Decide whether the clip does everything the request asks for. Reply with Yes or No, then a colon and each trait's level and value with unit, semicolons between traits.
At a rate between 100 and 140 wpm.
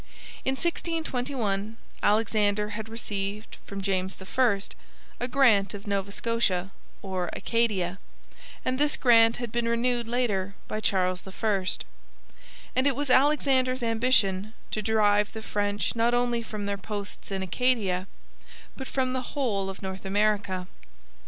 Yes: slow, 135 wpm